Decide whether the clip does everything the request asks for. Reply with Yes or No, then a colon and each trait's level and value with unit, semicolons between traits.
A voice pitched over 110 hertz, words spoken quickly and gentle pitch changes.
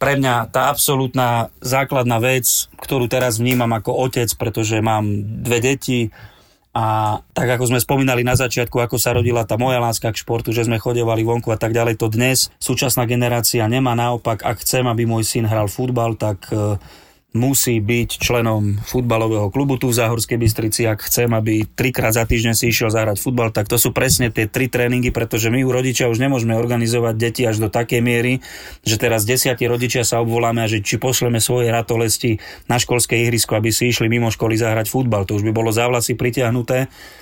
Yes: low, 120 Hz; fast, 190 wpm; narrow, 1.9 semitones